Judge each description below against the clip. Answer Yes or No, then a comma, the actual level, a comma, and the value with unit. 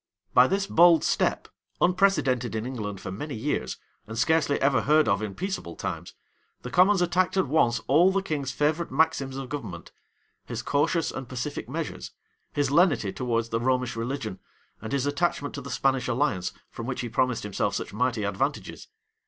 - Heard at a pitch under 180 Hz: Yes, low, 135 Hz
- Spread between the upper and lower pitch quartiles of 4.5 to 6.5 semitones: Yes, average, 5.3 semitones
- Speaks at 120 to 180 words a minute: Yes, average, 175 wpm